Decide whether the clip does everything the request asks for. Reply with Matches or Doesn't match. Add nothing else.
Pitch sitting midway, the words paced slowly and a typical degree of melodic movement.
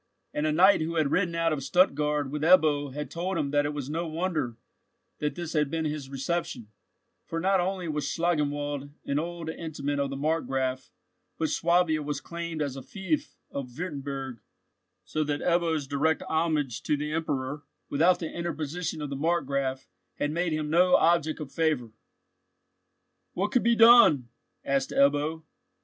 Doesn't match